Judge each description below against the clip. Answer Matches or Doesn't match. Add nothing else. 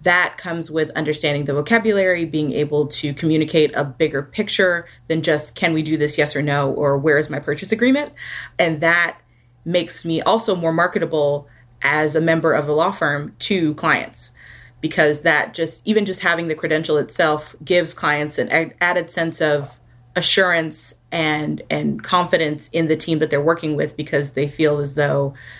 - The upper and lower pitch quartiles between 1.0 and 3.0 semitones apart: Matches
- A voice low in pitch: Doesn't match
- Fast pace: Doesn't match